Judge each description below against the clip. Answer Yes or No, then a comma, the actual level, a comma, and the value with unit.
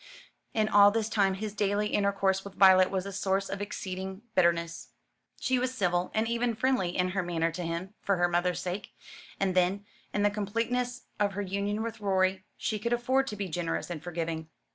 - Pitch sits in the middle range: No, high, 195 Hz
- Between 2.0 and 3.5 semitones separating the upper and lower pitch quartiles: Yes, narrow, 2.6 semitones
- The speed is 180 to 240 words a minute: Yes, average, 195 wpm